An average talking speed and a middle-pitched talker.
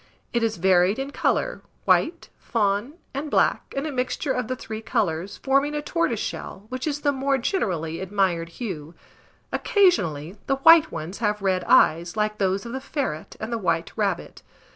No: average, 170 wpm; high, 220 Hz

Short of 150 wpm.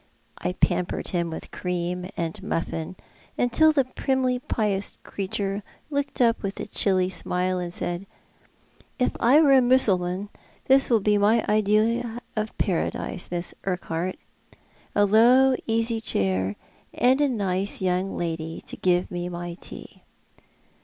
Yes: average, 140 wpm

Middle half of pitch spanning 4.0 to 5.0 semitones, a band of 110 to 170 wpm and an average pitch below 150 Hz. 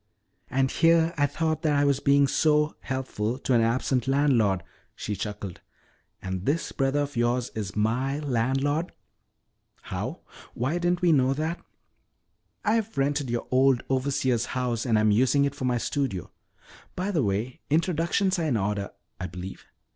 Yes: average, 4.4 semitones; average, 160 wpm; low, 135 Hz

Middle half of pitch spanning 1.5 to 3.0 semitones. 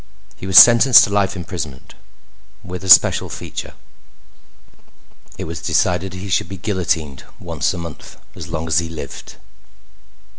Yes: average, 2.7 semitones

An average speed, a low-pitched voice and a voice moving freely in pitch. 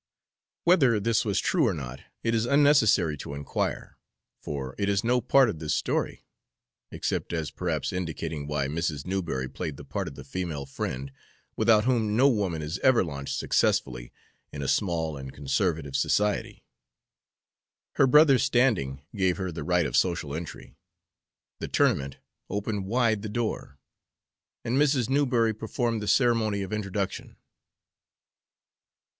Yes: average, 145 wpm; very low, 95 Hz; wide, 7.6 semitones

